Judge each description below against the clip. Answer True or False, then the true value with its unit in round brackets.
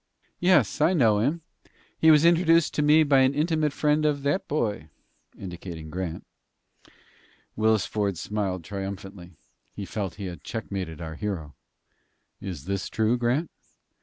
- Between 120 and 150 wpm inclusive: True (145 wpm)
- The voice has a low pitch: True (110 Hz)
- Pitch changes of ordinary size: False (8.1 semitones)